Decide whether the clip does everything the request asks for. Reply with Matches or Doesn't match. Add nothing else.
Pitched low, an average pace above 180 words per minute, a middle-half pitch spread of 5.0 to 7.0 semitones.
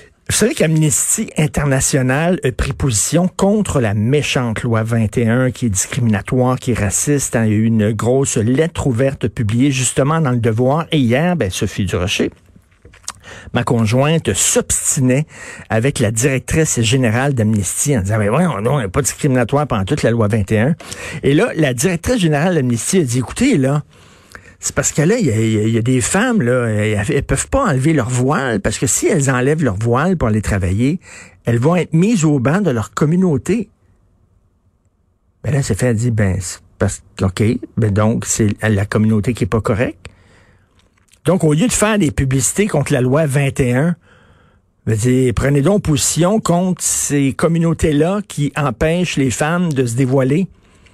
Doesn't match